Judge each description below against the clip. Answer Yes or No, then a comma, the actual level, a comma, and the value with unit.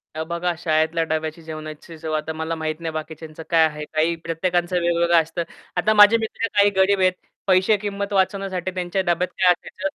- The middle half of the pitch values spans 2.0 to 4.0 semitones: Yes, average, 2.9 semitones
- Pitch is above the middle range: No, medium, 170 Hz